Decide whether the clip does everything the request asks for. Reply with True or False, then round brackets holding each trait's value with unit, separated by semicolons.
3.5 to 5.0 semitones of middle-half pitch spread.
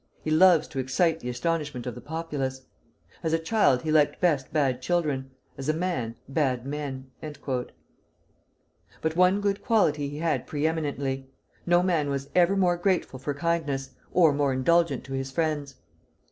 True (3.9 semitones)